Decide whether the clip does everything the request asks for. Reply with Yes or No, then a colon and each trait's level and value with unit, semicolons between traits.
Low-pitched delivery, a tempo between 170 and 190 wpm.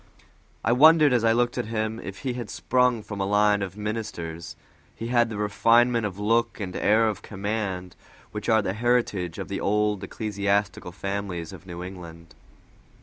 Yes: low, 105 Hz; average, 175 wpm